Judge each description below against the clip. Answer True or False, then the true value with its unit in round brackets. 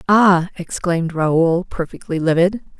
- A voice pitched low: False (175 Hz)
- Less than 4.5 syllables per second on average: True (4.3 syllables/s)